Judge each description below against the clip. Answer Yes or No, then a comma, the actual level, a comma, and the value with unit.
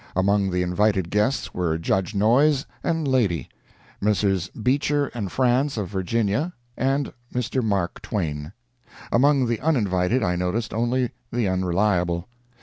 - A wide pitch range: Yes, wide, 5.7 semitones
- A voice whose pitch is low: Yes, low, 105 Hz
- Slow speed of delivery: Yes, slow, 130 wpm